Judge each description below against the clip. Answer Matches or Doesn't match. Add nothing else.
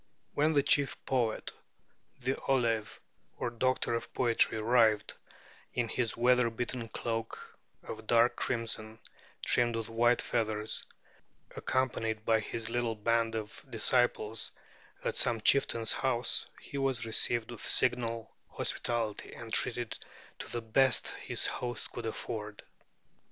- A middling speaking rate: Doesn't match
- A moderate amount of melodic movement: Doesn't match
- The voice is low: Matches